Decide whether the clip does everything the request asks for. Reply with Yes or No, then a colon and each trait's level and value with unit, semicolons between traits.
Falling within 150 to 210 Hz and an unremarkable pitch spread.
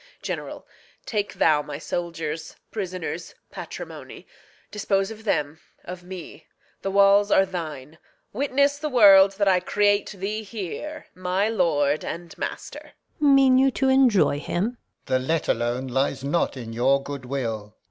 No: medium, 185 Hz; wide, 6.3 semitones